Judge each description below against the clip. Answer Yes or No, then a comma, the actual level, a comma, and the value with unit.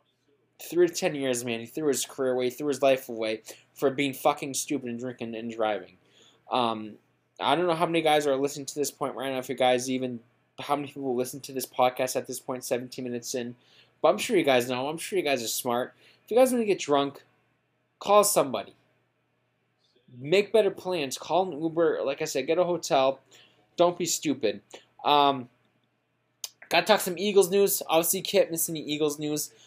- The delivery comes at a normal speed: No, fast, 210 wpm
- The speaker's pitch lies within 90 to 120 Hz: No, medium, 140 Hz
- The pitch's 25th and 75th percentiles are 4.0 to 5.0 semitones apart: Yes, average, 4.6 semitones